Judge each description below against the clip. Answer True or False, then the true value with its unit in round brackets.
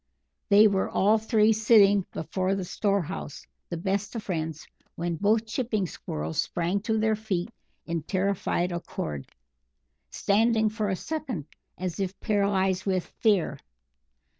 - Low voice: False (200 Hz)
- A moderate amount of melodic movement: True (3.4 semitones)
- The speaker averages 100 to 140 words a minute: True (135 wpm)